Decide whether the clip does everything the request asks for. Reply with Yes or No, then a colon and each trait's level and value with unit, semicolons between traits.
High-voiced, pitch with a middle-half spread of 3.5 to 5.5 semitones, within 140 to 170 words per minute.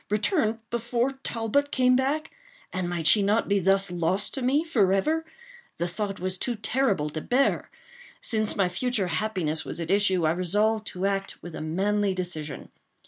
Yes: high, 205 Hz; average, 5.2 semitones; average, 165 wpm